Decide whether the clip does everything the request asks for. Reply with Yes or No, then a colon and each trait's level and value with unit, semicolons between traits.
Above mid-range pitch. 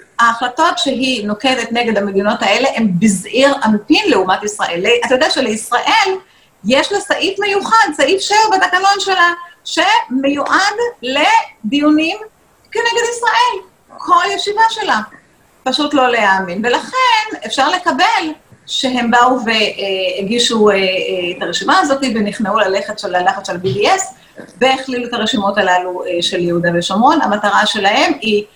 Yes: very high, 260 Hz